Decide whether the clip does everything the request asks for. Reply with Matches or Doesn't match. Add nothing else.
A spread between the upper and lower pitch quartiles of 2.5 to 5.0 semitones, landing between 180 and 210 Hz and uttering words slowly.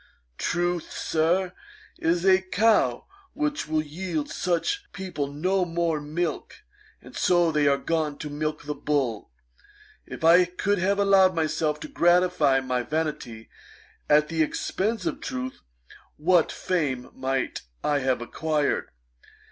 Doesn't match